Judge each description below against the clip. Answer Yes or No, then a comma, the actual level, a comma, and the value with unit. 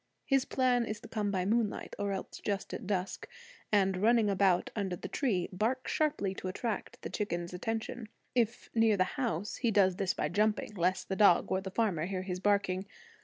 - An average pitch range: Yes, average, 3.3 semitones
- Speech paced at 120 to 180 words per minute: No, average, 195 wpm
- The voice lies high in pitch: Yes, high, 200 Hz